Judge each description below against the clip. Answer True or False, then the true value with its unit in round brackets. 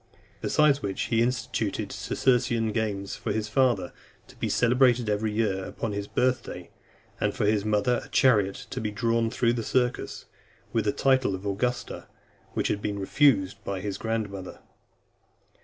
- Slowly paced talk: False (160 wpm)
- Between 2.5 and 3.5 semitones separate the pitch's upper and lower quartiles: True (3.2 semitones)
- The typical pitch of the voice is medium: False (110 Hz)